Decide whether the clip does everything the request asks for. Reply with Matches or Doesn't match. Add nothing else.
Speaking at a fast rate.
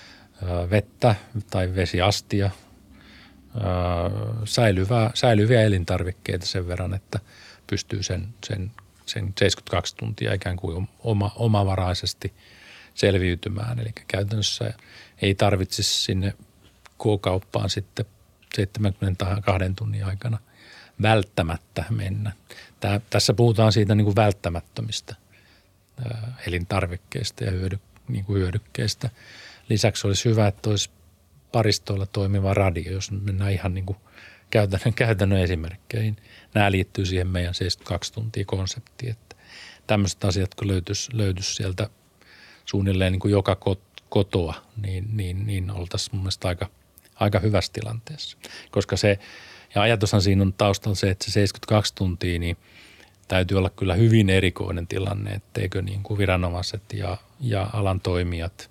Doesn't match